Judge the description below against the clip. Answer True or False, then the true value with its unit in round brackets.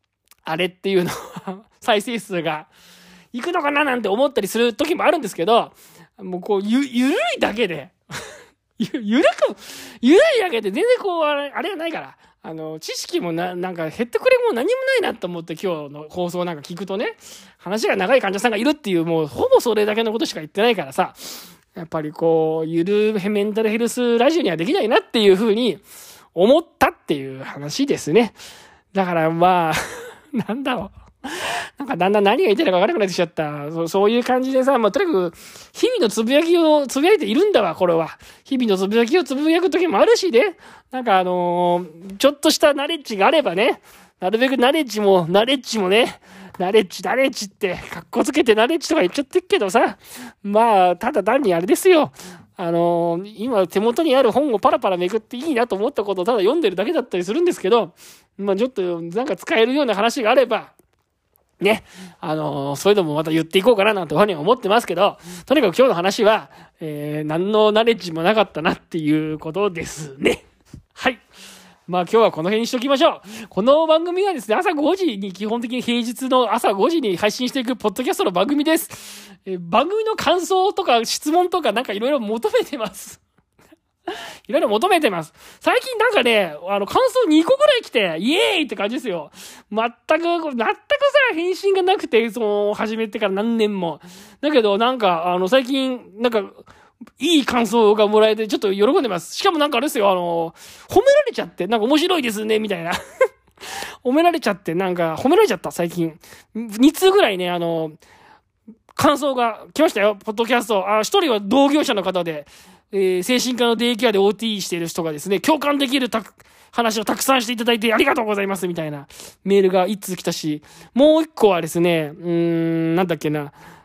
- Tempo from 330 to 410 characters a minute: True (400 characters per minute)